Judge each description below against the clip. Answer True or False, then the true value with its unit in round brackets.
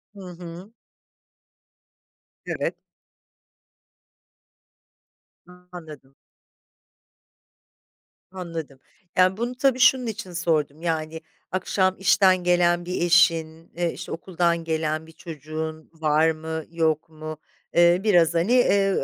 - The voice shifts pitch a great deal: False (2.5 semitones)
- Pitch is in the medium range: True (170 Hz)